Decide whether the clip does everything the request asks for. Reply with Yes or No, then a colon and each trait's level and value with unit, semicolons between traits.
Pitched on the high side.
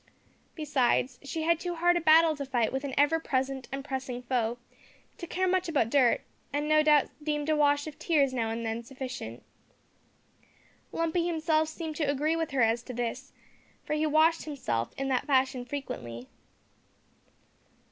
Yes: very high, 285 Hz